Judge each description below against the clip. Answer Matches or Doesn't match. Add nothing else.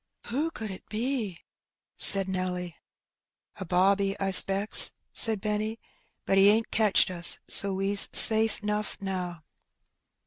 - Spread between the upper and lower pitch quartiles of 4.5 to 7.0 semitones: Doesn't match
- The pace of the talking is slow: Doesn't match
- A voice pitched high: Matches